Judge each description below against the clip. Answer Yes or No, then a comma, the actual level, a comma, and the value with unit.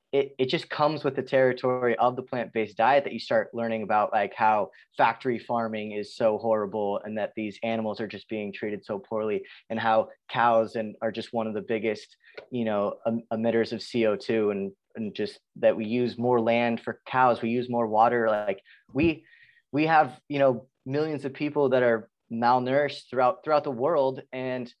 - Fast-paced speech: No, average, 195 wpm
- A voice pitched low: Yes, low, 120 Hz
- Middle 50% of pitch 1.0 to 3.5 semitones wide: Yes, average, 3.0 semitones